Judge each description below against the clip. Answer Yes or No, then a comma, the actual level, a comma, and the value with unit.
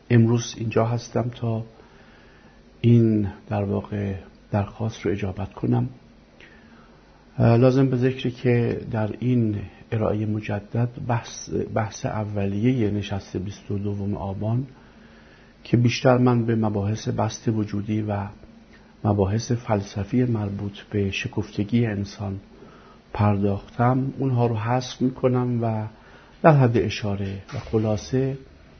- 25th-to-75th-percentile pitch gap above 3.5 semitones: No, average, 2.9 semitones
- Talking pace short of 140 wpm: Yes, average, 110 wpm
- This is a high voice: No, low, 110 Hz